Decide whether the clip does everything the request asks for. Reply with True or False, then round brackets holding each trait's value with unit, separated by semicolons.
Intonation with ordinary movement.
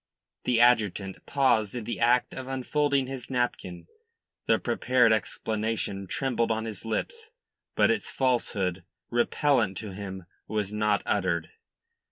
True (4.0 semitones)